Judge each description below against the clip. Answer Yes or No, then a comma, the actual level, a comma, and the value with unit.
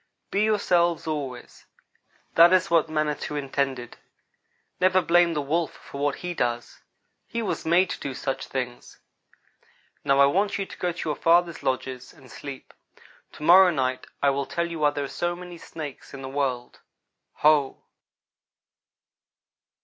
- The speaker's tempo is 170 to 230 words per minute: No, average, 155 wpm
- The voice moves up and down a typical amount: Yes, average, 4.2 semitones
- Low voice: No, medium, 150 Hz